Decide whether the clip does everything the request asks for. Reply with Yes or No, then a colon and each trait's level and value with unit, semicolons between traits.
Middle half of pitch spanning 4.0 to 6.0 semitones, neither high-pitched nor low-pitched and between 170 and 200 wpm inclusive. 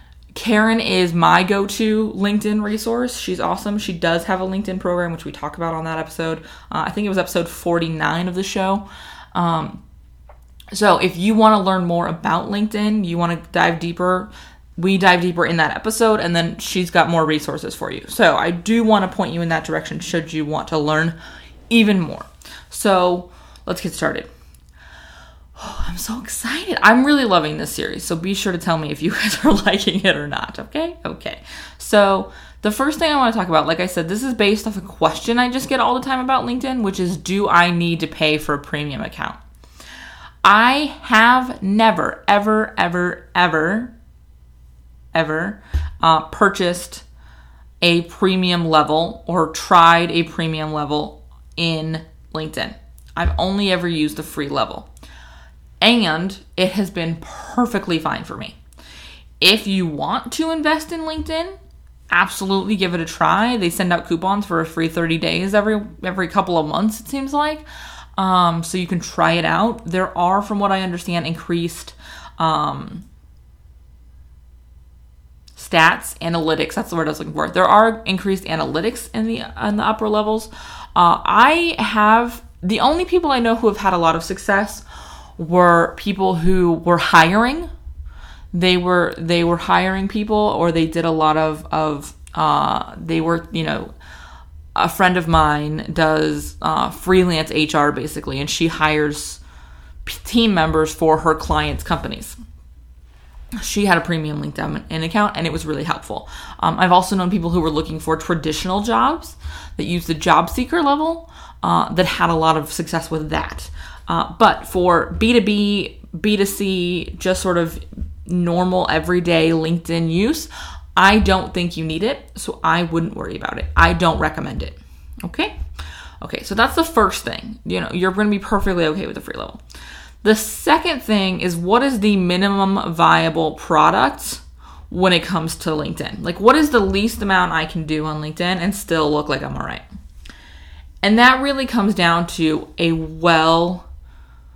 Yes: average, 4.7 semitones; medium, 175 Hz; average, 175 wpm